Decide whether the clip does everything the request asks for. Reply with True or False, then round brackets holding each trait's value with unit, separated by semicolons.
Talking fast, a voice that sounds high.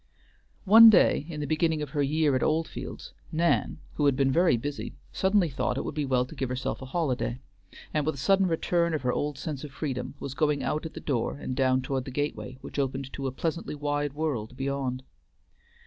False (215 wpm; 145 Hz)